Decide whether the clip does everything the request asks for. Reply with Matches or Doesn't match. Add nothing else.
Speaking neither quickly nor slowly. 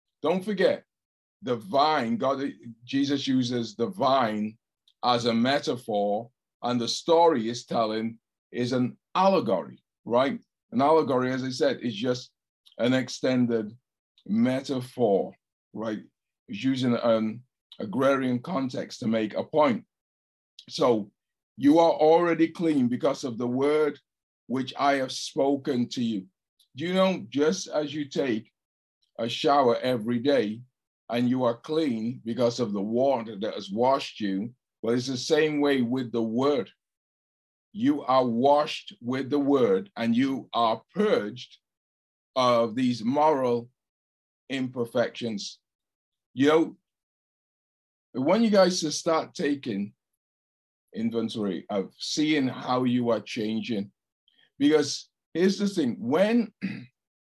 Doesn't match